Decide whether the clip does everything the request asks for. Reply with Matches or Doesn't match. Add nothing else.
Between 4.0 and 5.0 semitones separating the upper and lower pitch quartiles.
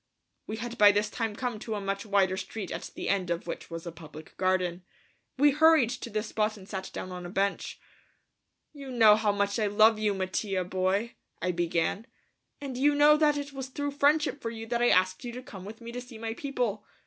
Matches